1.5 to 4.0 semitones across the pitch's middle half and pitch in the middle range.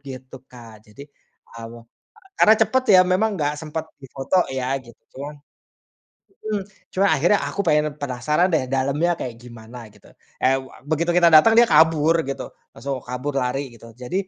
No: average, 5.3 semitones; medium, 145 Hz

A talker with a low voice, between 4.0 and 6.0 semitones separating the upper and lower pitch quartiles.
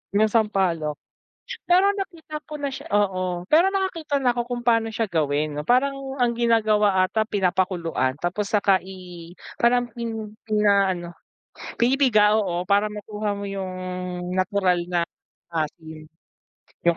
No: high, 205 Hz; average, 4.8 semitones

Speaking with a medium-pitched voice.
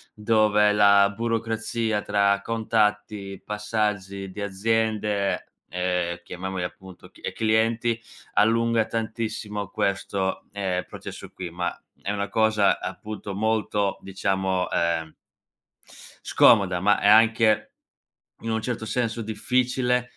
No: low, 105 Hz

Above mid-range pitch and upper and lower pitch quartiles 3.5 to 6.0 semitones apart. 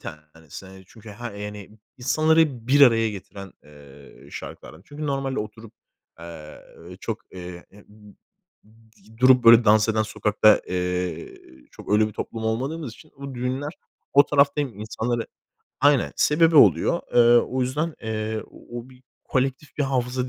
No: low, 115 Hz; average, 4.4 semitones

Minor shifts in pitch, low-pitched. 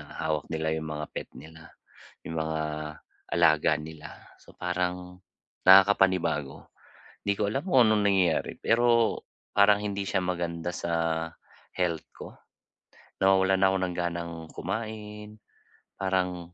No: average, 3.2 semitones; very low, 90 Hz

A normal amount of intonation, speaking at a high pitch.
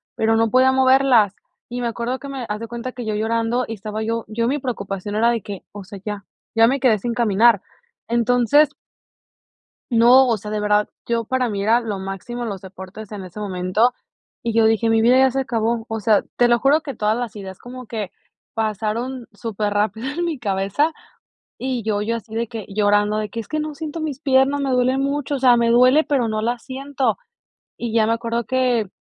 Yes: average, 3.2 semitones; high, 230 Hz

